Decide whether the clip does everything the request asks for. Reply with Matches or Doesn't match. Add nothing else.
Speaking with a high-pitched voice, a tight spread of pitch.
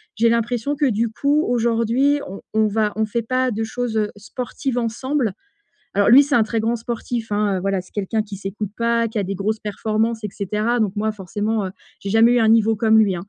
Matches